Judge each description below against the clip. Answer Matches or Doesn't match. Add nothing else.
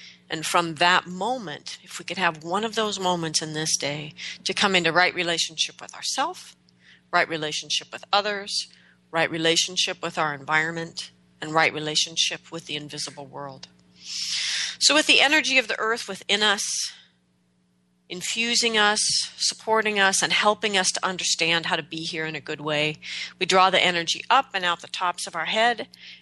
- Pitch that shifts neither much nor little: Matches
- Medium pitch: Matches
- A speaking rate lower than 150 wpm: Doesn't match